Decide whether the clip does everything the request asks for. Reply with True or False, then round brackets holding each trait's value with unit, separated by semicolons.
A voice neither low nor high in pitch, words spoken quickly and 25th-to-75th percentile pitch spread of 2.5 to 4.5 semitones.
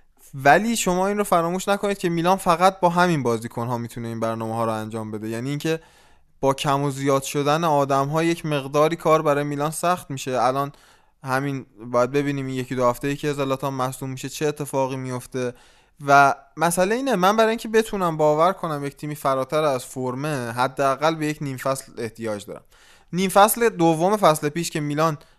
True (145 Hz; 190 wpm; 4.2 semitones)